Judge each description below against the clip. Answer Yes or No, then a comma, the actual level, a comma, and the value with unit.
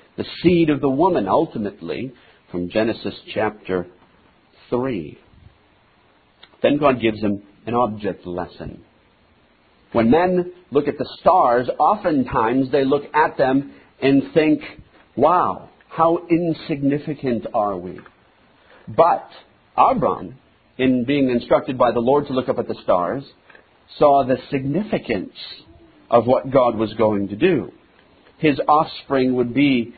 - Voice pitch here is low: Yes, low, 130 Hz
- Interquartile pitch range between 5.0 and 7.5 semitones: Yes, average, 5.3 semitones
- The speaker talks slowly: Yes, slow, 125 wpm